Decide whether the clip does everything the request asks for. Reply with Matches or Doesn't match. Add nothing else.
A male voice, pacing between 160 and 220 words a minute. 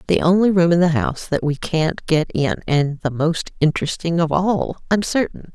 Doesn't match